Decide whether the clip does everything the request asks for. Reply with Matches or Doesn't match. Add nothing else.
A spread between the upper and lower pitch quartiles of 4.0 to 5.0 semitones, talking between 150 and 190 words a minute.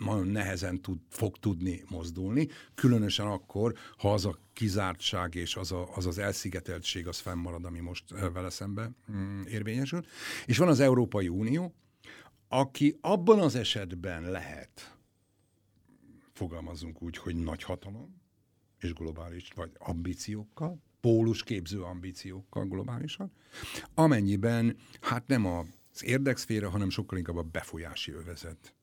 Doesn't match